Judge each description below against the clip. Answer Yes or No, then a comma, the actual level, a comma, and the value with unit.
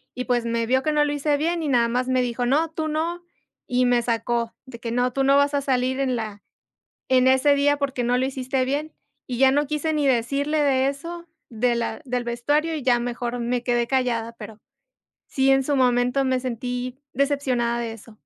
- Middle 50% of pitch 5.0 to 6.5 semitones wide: No, average, 2.8 semitones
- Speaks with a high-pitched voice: Yes, very high, 255 Hz